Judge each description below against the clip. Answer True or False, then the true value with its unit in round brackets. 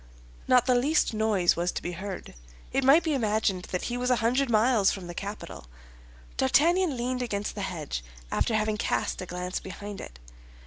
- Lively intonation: False (5.0 semitones)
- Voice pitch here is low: False (215 Hz)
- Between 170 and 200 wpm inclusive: True (185 wpm)